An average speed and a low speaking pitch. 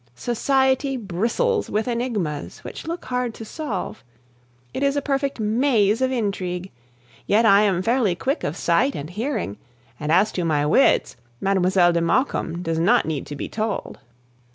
No: average, 160 wpm; high, 215 Hz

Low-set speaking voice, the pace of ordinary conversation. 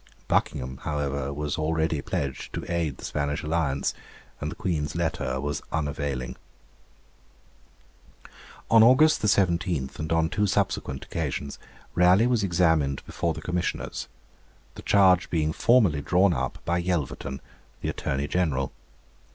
No: very low, 80 Hz; slow, 125 wpm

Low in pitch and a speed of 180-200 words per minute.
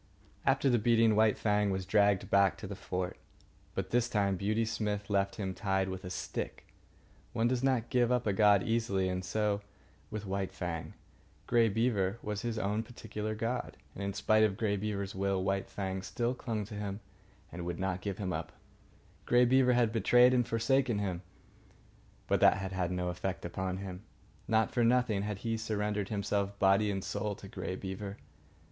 Yes: low, 105 Hz; average, 185 wpm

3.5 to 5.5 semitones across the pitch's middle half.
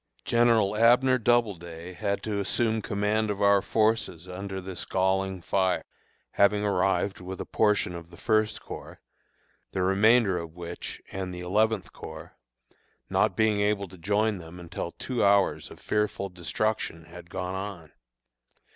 No: average, 2.9 semitones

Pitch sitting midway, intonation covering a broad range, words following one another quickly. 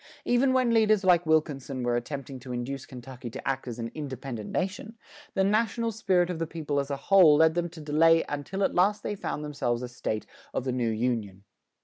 Yes: medium, 150 Hz; wide, 7.0 semitones; fast, 210 wpm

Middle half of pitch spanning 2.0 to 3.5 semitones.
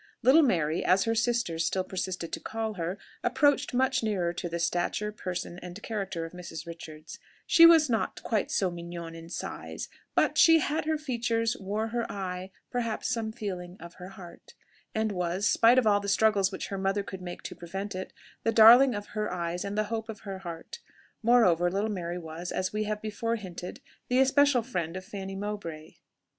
No: average, 4.3 semitones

